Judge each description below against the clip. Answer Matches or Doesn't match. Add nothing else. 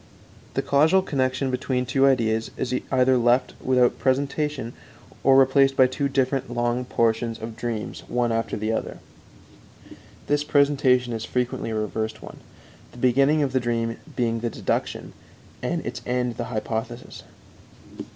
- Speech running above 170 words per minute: Doesn't match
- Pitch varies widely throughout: Doesn't match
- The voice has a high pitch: Doesn't match